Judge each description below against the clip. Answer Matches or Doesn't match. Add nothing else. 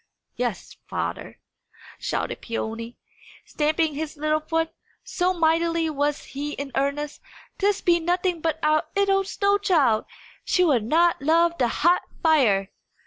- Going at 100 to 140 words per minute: Matches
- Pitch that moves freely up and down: Doesn't match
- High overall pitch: Matches